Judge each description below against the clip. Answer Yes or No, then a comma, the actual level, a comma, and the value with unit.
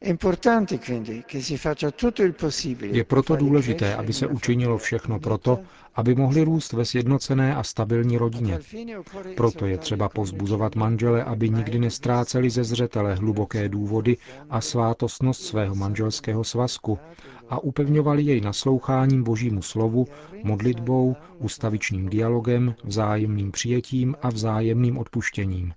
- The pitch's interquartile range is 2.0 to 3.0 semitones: No, average, 3.5 semitones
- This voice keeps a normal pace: No, slow, 110 wpm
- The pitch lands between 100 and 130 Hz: Yes, low, 120 Hz